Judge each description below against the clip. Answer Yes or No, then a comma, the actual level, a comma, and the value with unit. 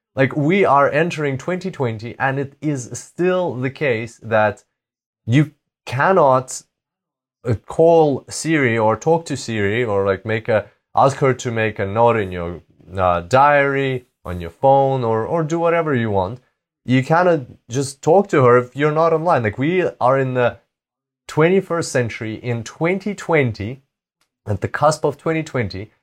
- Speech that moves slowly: No, average, 155 wpm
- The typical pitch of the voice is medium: No, low, 130 Hz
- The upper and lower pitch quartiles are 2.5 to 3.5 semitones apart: No, average, 5.3 semitones